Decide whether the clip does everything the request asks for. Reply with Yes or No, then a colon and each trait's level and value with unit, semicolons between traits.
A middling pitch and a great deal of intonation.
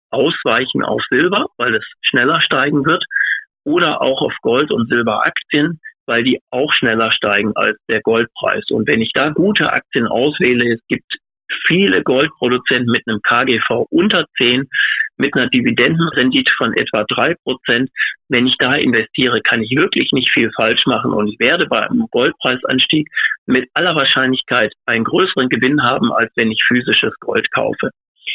No: low, 130 Hz; wide, 6.4 semitones